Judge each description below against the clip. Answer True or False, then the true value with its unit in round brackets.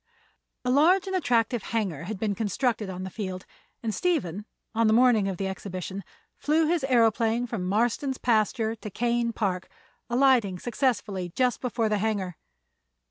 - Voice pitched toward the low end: False (225 Hz)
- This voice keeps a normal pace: True (155 wpm)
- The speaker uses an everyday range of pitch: True (4.0 semitones)